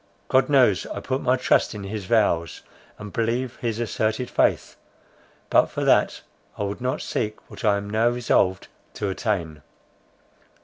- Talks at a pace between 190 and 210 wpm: No, average, 150 wpm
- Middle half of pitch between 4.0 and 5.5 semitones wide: No, average, 3.4 semitones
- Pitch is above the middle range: No, low, 110 Hz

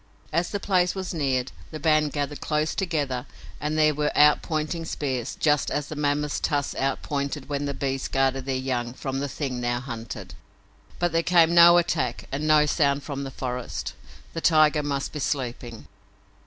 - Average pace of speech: Yes, average, 175 wpm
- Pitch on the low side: No, medium, 145 Hz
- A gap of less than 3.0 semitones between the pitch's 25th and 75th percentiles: Yes, narrow, 2.5 semitones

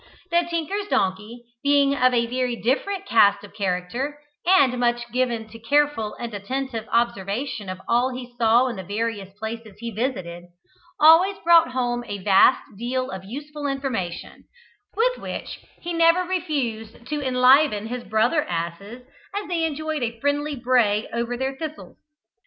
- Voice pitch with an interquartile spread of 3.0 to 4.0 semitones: No, average, 4.7 semitones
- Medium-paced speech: Yes, average, 150 wpm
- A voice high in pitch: Yes, high, 245 Hz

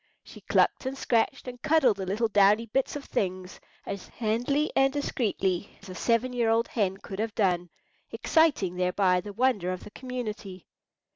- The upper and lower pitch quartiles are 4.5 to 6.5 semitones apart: Yes, average, 4.9 semitones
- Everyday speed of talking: Yes, average, 170 wpm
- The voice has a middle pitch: No, high, 215 Hz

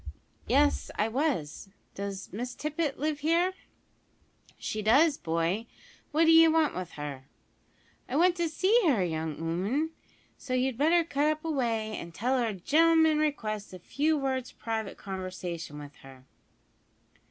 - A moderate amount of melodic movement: No, wide, 8.6 semitones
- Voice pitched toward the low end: No, very high, 250 Hz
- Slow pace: No, average, 145 wpm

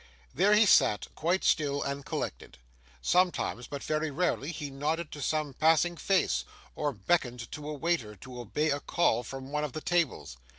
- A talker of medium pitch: Yes, medium, 150 Hz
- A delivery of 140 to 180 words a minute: Yes, average, 175 wpm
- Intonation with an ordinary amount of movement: Yes, average, 3.9 semitones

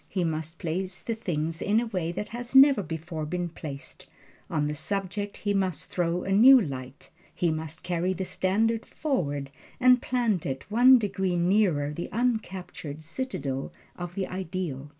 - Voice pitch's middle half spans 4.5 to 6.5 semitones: Yes, average, 4.9 semitones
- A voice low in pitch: No, medium, 180 Hz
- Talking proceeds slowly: No, average, 165 wpm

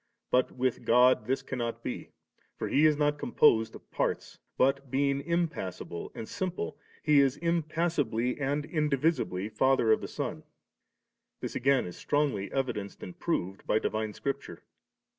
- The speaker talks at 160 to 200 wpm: No, average, 150 wpm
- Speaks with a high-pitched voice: No, low, 135 Hz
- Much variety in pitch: No, average, 4.7 semitones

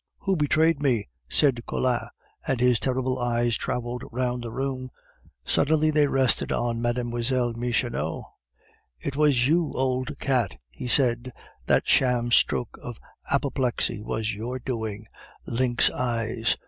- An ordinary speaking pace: No, slow, 130 wpm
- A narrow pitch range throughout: Yes, narrow, 2.1 semitones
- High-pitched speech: No, low, 125 Hz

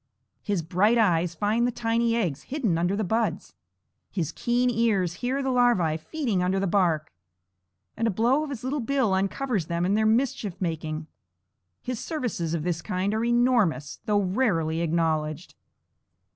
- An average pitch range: No, wide, 6.0 semitones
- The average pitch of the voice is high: Yes, high, 205 Hz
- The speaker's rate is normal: Yes, average, 160 wpm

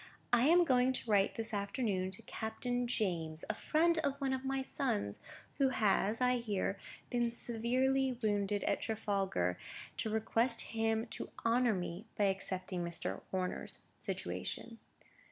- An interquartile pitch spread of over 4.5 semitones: No, average, 4.2 semitones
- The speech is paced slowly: No, average, 145 wpm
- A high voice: Yes, high, 225 Hz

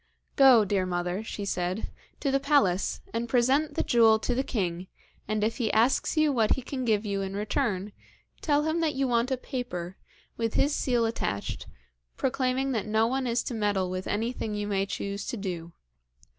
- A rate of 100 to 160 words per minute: No, average, 190 wpm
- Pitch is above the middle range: Yes, high, 225 Hz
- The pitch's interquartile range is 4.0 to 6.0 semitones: Yes, average, 4.7 semitones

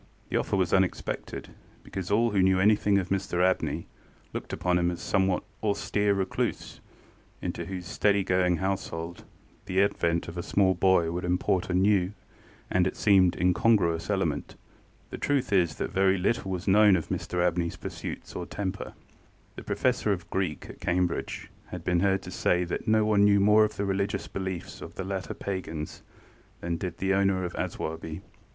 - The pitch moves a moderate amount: No, narrow, 1.9 semitones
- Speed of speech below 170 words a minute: No, average, 175 wpm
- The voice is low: Yes, very low, 95 Hz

